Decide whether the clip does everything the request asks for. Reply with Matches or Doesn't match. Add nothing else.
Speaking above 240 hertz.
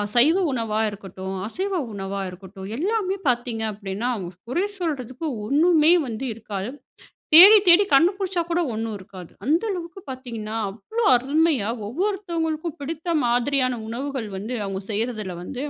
Matches